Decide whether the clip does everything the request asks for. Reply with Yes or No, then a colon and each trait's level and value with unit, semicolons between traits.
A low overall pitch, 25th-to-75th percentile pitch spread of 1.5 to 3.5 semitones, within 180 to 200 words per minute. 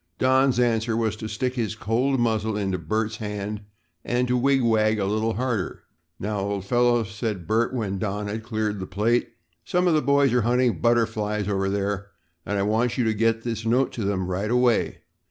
Yes: low, 110 Hz; average, 2.9 semitones; average, 195 wpm